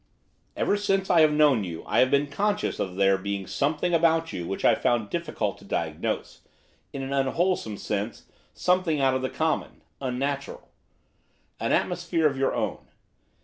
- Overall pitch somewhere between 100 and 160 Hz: Yes, medium, 140 Hz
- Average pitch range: No, wide, 7.7 semitones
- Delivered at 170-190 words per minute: Yes, average, 175 wpm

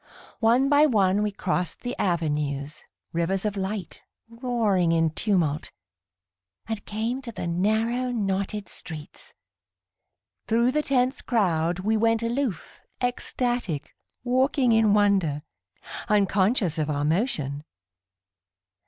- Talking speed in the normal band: No, slow, 110 wpm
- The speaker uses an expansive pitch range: Yes, wide, 5.7 semitones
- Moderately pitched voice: No, high, 205 Hz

